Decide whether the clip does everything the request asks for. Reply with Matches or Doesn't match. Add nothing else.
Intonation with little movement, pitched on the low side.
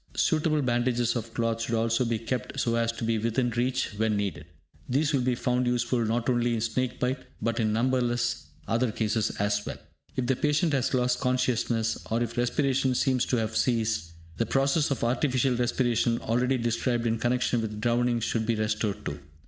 Matches